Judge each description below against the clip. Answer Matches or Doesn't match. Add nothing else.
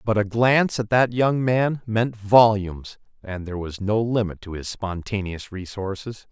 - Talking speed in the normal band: Matches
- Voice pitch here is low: Matches